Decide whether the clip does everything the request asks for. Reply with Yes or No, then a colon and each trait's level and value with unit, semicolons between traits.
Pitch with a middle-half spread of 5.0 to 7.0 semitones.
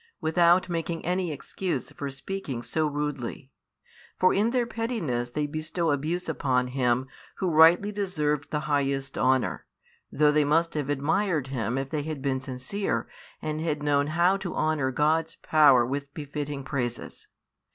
No: average, 3.6 semitones